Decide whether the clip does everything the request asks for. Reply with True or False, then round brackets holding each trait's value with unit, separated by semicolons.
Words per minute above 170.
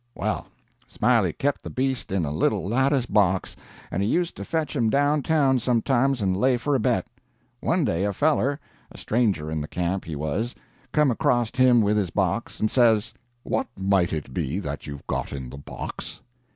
True (190 wpm)